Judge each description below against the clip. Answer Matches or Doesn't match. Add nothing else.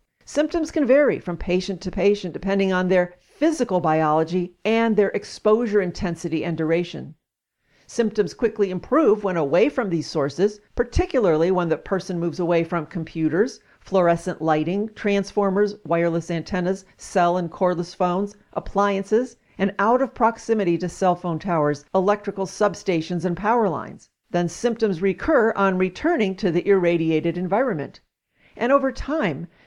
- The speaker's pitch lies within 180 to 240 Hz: Matches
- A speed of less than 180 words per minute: Matches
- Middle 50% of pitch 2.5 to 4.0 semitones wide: Matches